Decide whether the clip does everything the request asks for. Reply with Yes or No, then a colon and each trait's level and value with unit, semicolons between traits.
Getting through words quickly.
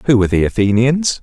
No: average, 195 wpm